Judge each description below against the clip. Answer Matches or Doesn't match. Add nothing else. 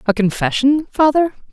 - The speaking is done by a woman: Matches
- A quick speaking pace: Doesn't match